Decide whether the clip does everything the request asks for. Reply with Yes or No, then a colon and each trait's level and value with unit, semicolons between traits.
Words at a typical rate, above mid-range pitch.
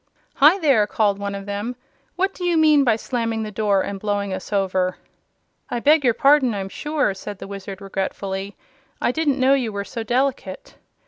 Yes: average, 190 wpm; high, 215 Hz